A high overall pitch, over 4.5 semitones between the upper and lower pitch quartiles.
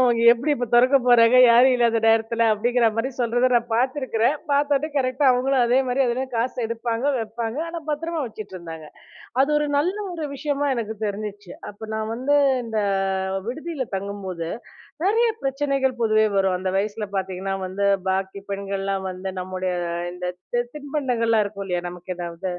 Yes: high, 230 Hz; average, 4.9 semitones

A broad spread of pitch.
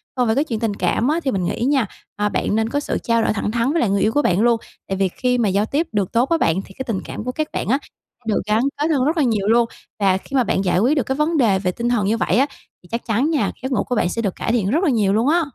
No: average, 4.6 semitones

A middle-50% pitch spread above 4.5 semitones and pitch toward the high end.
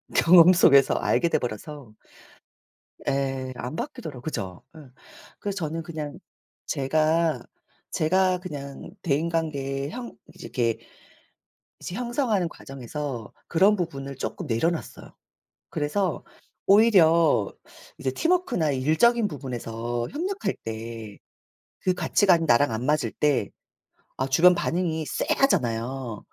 No: wide, 5.5 semitones; medium, 155 Hz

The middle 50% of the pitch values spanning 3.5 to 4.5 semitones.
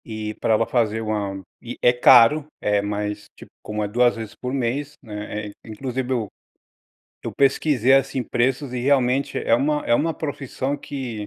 Yes: average, 3.9 semitones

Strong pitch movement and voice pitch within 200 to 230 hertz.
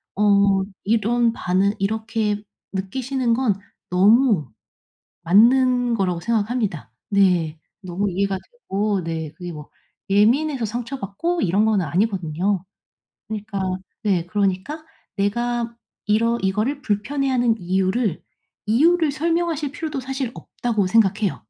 No: average, 4.3 semitones; high, 210 Hz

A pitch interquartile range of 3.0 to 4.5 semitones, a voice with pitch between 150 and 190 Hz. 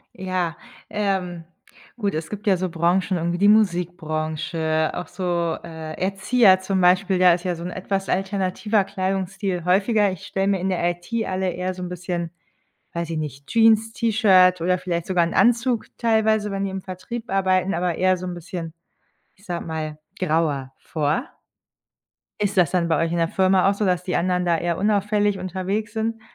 No: narrow, 2.4 semitones; medium, 185 Hz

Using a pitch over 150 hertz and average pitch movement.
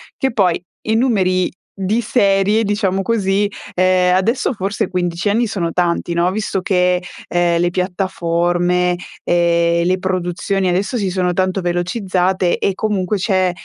No: medium, 185 Hz; narrow, 2.0 semitones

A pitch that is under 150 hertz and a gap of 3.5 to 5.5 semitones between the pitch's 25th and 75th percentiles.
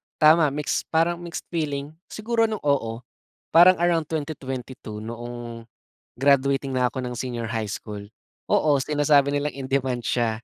Yes: medium, 140 Hz; average, 4.3 semitones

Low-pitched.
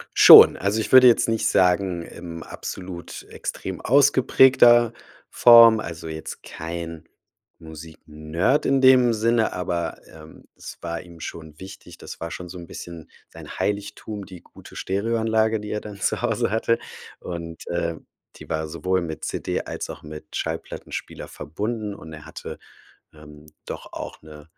Yes: very low, 90 Hz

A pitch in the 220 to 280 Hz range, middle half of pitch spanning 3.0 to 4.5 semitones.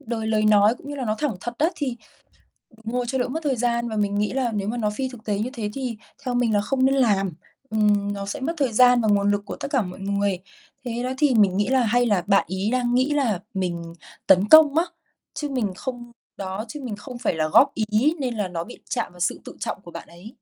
Yes: high, 225 Hz; average, 4.0 semitones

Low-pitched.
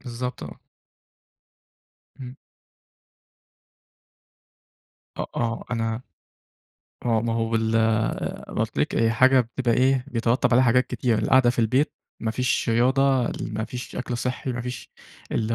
Yes: low, 120 Hz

